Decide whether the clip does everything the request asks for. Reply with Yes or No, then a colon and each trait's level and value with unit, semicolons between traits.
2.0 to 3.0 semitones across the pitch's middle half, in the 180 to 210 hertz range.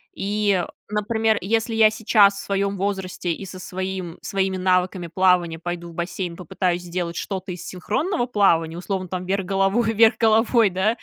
Yes: average, 2.7 semitones; high, 190 Hz